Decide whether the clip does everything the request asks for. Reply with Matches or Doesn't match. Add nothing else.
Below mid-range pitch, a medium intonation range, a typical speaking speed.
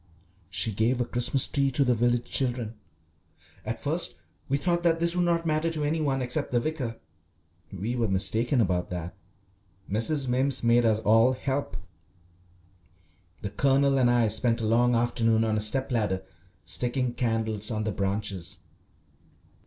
Matches